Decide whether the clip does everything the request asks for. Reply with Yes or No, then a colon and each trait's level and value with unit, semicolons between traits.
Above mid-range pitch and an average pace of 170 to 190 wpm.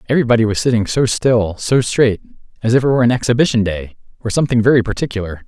No: low, 115 Hz; average, 185 wpm